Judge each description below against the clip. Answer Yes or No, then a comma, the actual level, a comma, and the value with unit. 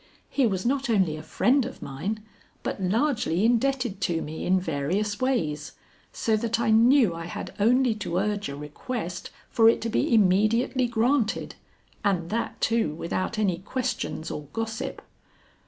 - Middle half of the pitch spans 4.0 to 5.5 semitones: Yes, average, 5.1 semitones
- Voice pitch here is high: Yes, high, 215 Hz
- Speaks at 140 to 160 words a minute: Yes, average, 155 wpm